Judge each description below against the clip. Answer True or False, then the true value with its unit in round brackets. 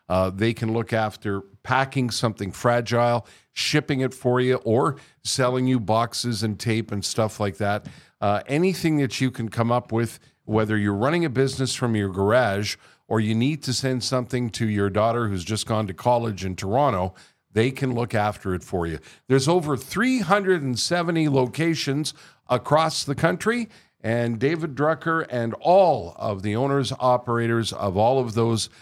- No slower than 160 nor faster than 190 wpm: True (170 wpm)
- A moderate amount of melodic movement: True (4.2 semitones)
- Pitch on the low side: True (120 Hz)